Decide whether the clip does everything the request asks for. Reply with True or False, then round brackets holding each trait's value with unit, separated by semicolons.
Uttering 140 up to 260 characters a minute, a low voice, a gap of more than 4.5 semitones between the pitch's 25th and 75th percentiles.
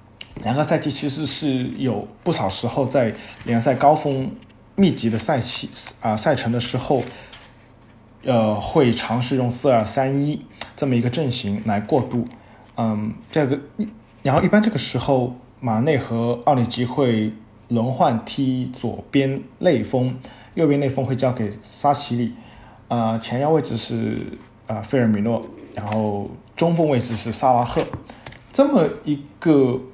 False (220 characters per minute; 125 Hz; 3.9 semitones)